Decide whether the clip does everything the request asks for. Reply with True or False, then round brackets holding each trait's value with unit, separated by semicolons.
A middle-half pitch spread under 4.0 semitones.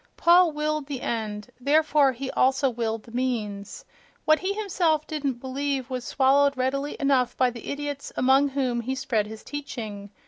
True (3.2 semitones)